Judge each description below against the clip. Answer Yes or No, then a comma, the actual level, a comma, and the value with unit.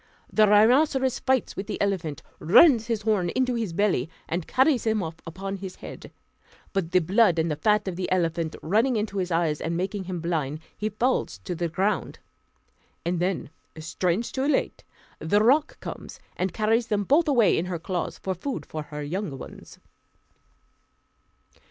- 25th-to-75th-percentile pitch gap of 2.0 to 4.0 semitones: No, average, 4.8 semitones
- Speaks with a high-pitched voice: Yes, high, 195 Hz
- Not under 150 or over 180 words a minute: Yes, average, 175 wpm